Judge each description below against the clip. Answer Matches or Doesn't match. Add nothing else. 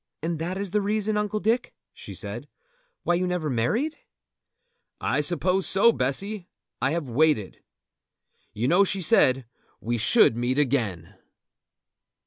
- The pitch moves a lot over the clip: Matches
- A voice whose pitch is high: Doesn't match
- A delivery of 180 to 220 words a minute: Doesn't match